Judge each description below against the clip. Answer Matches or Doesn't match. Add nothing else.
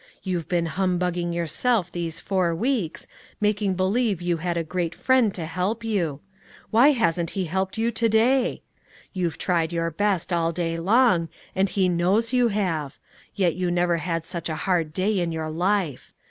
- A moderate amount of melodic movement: Matches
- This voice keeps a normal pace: Matches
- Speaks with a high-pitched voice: Doesn't match